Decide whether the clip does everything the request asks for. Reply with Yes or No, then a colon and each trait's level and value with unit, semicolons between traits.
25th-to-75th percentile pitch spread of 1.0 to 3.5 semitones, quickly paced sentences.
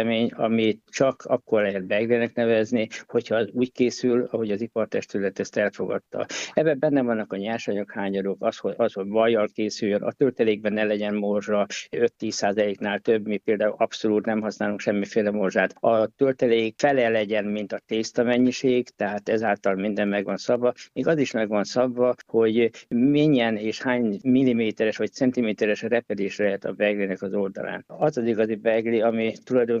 Yes: narrow, 2.5 semitones; fast, 165 wpm